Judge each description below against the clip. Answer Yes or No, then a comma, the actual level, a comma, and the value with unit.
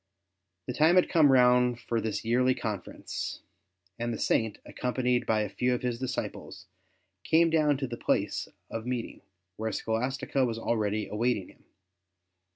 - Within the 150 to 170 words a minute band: Yes, average, 155 wpm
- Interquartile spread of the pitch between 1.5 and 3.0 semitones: Yes, narrow, 2.5 semitones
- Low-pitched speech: Yes, low, 125 Hz